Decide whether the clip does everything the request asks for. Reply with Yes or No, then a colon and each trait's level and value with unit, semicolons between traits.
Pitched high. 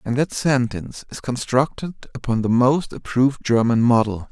No: low, 125 Hz